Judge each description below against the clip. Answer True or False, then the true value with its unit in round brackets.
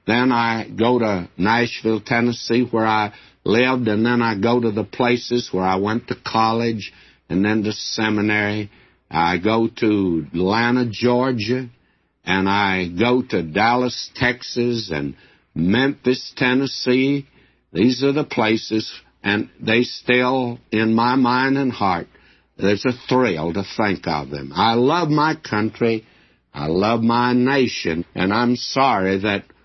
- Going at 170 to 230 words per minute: False (140 wpm)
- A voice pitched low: True (115 Hz)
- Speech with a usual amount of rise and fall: True (3.5 semitones)